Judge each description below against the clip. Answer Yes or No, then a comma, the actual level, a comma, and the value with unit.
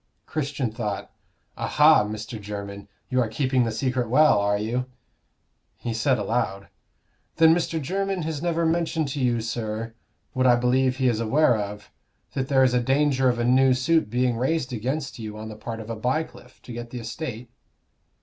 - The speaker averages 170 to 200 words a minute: Yes, average, 180 wpm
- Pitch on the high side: No, low, 125 Hz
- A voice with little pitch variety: No, average, 3.7 semitones